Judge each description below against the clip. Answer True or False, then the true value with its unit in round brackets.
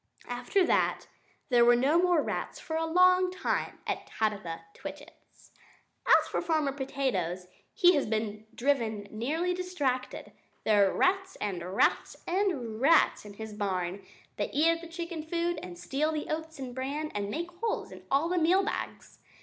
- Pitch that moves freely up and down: True (7.6 semitones)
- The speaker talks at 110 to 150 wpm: False (165 wpm)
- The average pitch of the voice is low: False (280 Hz)